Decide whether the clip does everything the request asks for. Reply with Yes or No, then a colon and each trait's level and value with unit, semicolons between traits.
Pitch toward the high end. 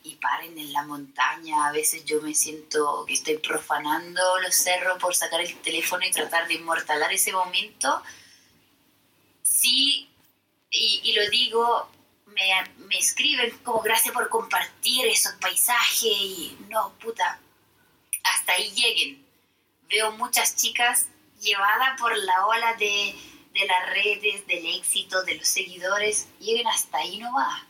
Yes: high, 205 Hz